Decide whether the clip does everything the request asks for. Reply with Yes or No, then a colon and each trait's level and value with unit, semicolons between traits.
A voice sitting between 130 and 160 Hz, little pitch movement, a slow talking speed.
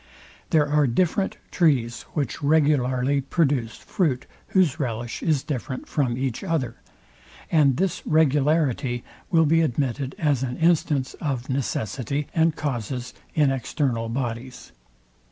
No: medium, 140 Hz; average, 3.7 semitones; slow, 120 wpm